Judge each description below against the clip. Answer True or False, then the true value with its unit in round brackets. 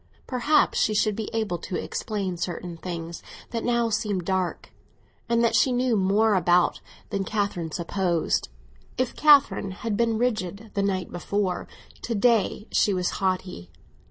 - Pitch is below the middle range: False (200 Hz)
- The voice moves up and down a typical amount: True (3.8 semitones)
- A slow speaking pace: False (150 wpm)